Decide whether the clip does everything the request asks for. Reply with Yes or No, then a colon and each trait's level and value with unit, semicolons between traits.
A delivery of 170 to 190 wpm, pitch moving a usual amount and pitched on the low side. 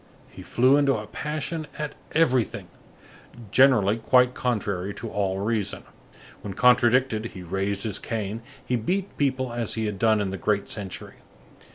No: average, 155 wpm; average, 4.2 semitones; low, 115 Hz